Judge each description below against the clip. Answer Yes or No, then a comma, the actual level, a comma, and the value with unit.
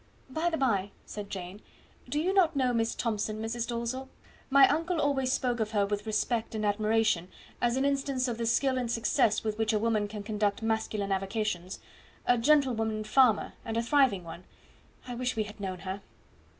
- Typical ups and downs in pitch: Yes, average, 3.6 semitones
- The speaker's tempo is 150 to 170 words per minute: No, average, 190 wpm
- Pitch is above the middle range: Yes, high, 225 Hz